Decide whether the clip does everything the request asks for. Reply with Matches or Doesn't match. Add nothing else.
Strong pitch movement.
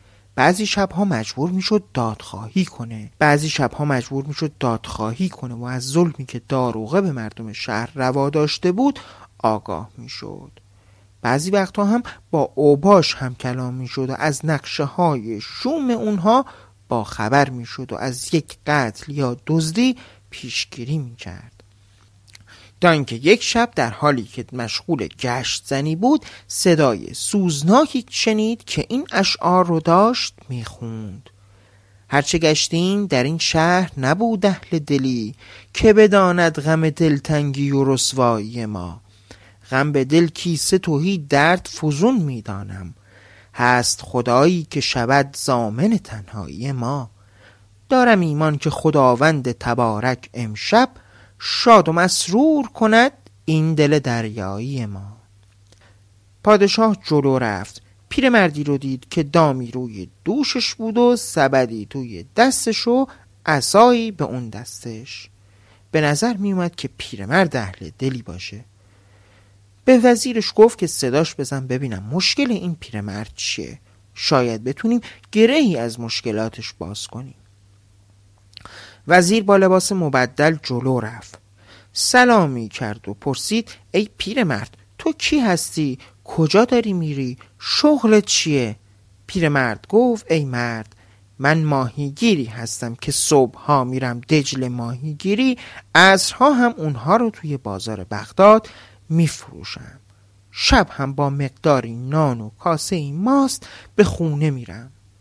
Matches